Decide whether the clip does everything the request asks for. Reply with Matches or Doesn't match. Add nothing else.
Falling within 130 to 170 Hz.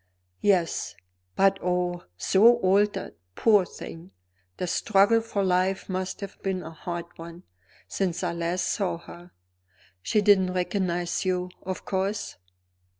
Doesn't match